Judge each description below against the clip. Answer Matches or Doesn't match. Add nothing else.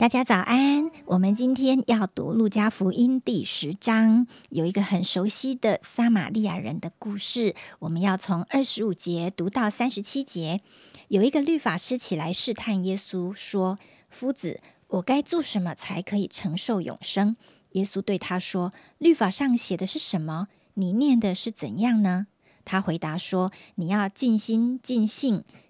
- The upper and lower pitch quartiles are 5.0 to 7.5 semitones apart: Doesn't match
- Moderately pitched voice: Doesn't match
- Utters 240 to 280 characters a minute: Matches